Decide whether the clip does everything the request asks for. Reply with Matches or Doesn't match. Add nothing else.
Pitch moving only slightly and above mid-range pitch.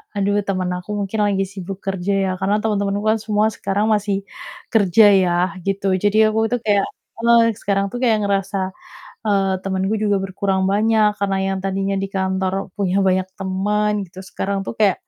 Matches